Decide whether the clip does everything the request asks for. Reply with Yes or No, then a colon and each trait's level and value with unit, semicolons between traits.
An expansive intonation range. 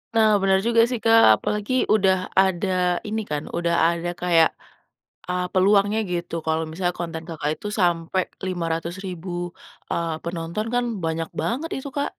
No: average, 3.4 semitones